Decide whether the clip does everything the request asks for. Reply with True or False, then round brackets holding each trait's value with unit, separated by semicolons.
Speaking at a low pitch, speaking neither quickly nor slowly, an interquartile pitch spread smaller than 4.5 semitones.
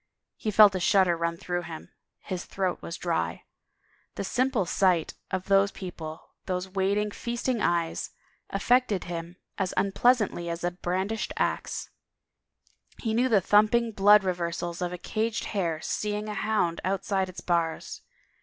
False (190 Hz; 155 wpm; 3.3 semitones)